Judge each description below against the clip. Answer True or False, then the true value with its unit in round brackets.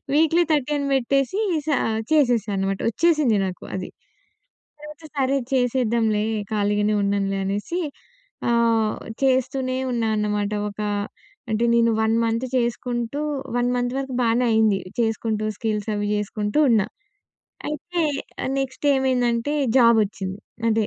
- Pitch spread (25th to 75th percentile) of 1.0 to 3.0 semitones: False (3.9 semitones)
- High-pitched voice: True (235 Hz)